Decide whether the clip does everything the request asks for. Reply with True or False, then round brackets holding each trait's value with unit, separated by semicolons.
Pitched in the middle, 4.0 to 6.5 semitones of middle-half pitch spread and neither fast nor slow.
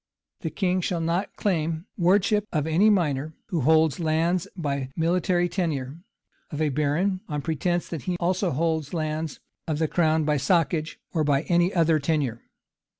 False (160 Hz; 2.5 semitones; 160 wpm)